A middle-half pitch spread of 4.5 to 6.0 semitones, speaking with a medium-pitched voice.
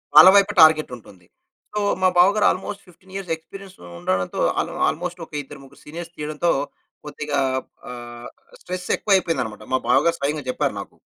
Yes: average, 5.1 semitones; medium, 160 Hz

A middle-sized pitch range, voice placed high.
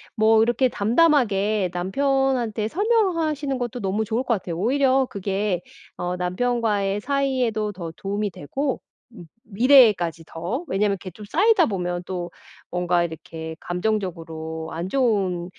No: wide, 6.2 semitones; high, 210 Hz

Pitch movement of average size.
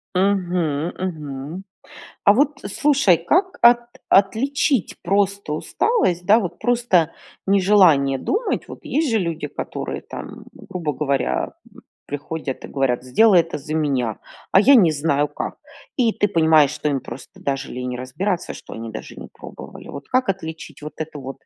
No: wide, 6.1 semitones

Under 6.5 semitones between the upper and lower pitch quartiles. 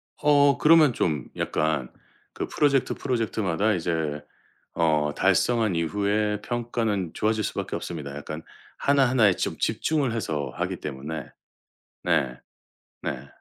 No: wide, 7.5 semitones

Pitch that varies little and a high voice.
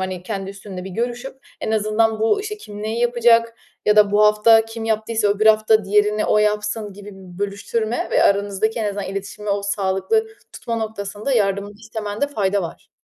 Yes: narrow, 1.9 semitones; high, 210 Hz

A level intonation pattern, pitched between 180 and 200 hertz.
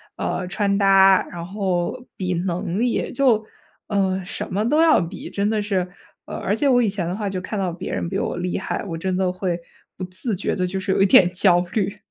Yes: narrow, 2.2 semitones; high, 190 Hz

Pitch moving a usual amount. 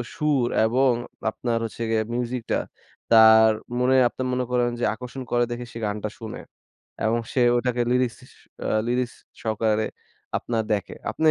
No: narrow, 2.1 semitones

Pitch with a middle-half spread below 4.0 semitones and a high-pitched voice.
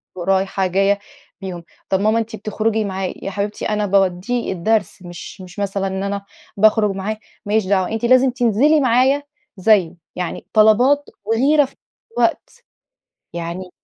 Yes: average, 2.9 semitones; high, 205 Hz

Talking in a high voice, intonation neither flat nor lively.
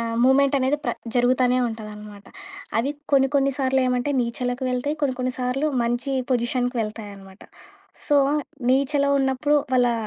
No: very high, 255 Hz; narrow, 2.3 semitones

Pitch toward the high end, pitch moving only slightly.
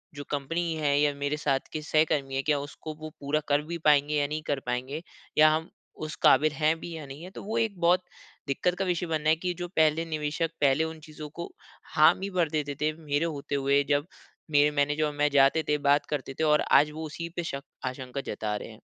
No: medium, 150 Hz; narrow, 2.1 semitones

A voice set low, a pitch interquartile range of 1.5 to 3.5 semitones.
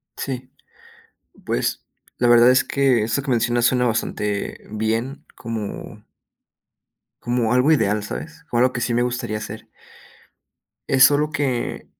Yes: low, 120 Hz; narrow, 2.6 semitones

